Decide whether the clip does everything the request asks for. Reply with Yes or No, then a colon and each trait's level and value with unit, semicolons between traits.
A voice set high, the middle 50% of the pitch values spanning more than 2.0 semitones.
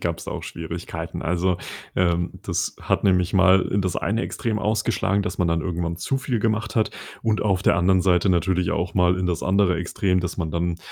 No: very low, 90 Hz; narrow, 2.4 semitones